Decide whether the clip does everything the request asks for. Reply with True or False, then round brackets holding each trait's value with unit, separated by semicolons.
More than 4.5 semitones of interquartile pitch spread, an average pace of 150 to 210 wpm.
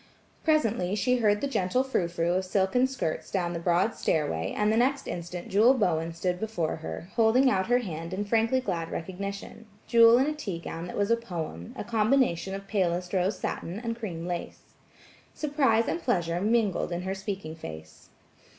True (5.0 semitones; 180 wpm)